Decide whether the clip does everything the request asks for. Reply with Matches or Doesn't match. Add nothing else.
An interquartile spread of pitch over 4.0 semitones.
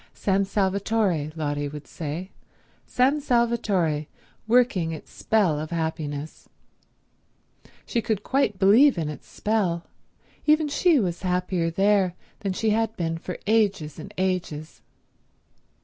Matches